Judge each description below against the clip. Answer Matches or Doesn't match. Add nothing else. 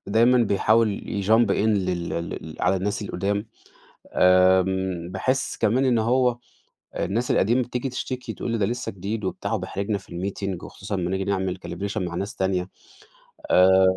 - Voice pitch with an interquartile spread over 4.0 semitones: Doesn't match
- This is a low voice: Matches